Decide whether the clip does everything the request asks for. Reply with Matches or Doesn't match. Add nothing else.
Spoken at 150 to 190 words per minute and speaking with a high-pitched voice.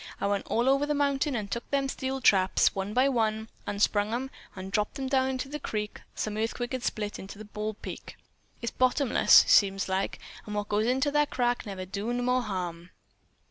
Doesn't match